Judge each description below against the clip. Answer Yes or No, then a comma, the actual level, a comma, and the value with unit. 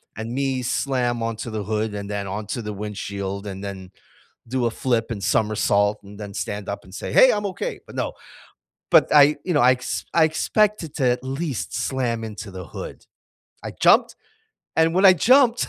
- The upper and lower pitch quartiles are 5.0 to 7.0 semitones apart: Yes, wide, 5.4 semitones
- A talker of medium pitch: No, low, 115 Hz